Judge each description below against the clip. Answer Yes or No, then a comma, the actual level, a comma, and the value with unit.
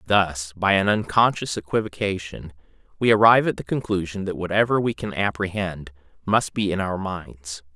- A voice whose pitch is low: Yes, very low, 95 Hz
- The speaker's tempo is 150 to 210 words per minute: Yes, average, 155 wpm